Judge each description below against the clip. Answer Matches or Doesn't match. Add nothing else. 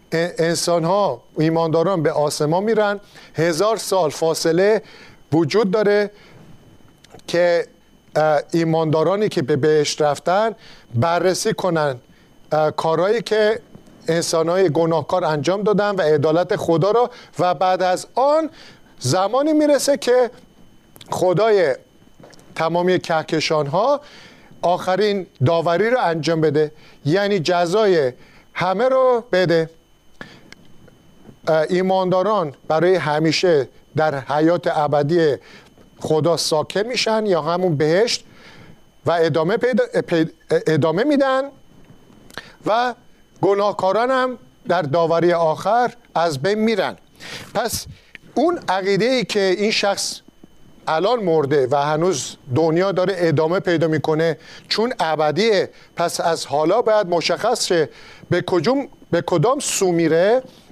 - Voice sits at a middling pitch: Matches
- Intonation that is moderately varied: Matches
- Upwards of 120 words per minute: Doesn't match